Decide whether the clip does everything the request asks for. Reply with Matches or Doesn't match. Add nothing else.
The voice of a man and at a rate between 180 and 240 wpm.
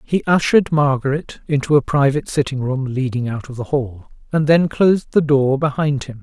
Matches